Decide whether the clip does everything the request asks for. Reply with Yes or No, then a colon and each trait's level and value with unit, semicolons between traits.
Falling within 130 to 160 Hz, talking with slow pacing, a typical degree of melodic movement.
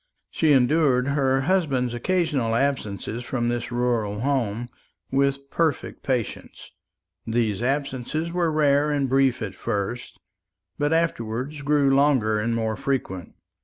Yes: low, 135 Hz; slow, 125 wpm; average, 3.6 semitones